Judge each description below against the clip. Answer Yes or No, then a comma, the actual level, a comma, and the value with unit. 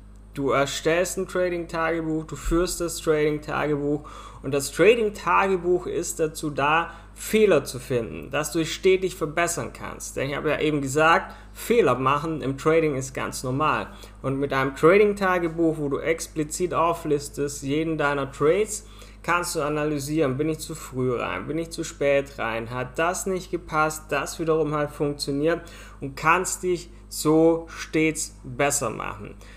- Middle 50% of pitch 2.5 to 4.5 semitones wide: Yes, average, 3.1 semitones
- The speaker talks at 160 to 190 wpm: No, average, 150 wpm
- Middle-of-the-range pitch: Yes, medium, 155 Hz